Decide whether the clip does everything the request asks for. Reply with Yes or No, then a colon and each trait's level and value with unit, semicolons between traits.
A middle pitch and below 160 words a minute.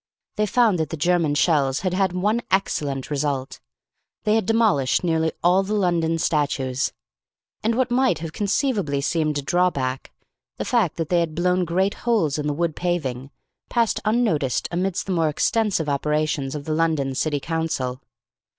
No: medium, 165 Hz; average, 170 wpm